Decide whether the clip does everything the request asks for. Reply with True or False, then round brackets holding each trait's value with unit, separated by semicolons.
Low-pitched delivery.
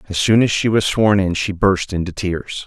True (95 Hz)